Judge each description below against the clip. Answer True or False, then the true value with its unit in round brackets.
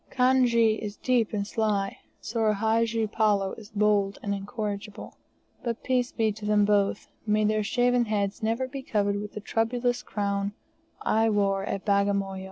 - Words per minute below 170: True (160 wpm)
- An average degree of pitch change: False (2.1 semitones)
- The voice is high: True (215 Hz)